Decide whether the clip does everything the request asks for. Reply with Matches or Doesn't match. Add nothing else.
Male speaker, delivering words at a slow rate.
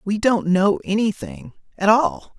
Matches